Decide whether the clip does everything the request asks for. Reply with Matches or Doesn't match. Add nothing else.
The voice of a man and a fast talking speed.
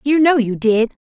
Doesn't match